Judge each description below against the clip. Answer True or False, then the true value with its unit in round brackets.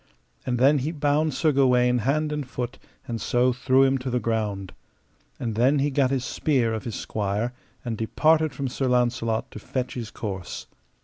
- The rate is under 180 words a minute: False (185 wpm)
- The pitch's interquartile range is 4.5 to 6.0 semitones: False (3.2 semitones)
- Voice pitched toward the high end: False (125 Hz)